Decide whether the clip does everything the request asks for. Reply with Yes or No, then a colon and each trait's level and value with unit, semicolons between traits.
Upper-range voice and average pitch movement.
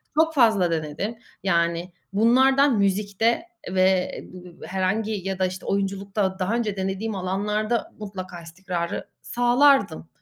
Yes: high, 195 Hz; average, 3.3 semitones